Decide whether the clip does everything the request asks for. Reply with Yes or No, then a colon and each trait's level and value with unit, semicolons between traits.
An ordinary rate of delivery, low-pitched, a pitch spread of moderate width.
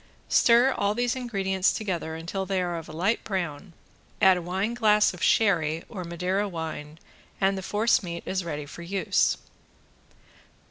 No: average, 165 wpm; high, 190 Hz; average, 3.4 semitones